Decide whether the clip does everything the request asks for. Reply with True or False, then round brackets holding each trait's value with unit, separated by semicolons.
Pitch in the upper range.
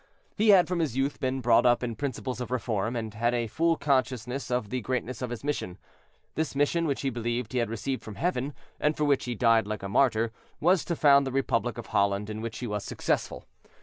False (125 Hz)